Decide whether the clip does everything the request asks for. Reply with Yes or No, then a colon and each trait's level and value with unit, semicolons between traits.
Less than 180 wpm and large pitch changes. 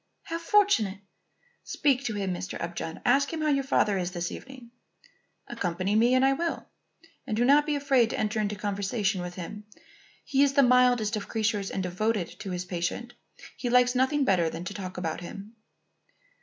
No: average, 185 wpm; wide, 5.8 semitones